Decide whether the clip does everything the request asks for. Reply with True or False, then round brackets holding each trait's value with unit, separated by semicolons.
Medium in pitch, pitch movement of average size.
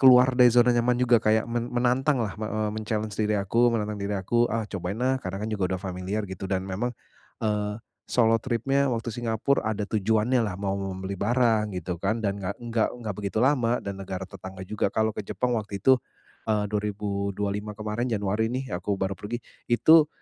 False (110 Hz; 3.2 semitones)